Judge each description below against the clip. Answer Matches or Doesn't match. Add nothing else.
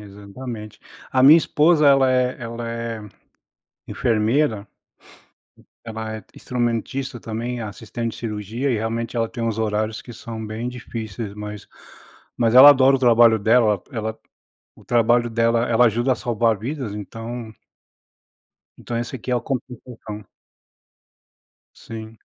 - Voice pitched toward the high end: Doesn't match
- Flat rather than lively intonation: Matches